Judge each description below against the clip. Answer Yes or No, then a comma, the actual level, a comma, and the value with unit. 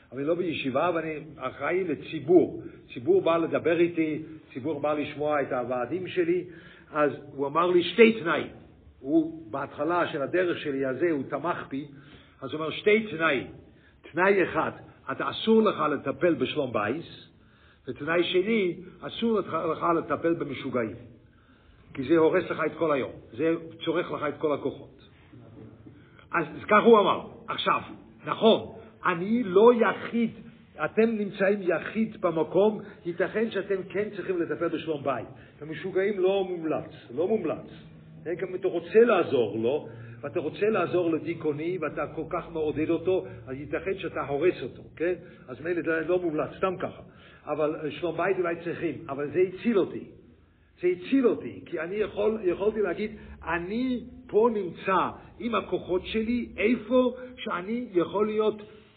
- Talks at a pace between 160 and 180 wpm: No, average, 150 wpm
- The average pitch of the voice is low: No, medium, 170 Hz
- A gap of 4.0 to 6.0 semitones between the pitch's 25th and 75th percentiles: Yes, average, 4.8 semitones